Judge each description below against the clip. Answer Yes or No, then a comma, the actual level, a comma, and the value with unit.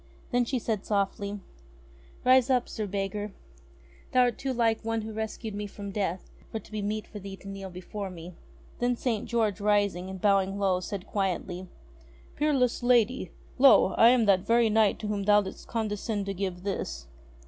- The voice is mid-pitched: No, high, 205 Hz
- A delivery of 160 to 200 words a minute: Yes, average, 190 wpm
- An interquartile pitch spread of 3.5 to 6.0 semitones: No, average, 2.8 semitones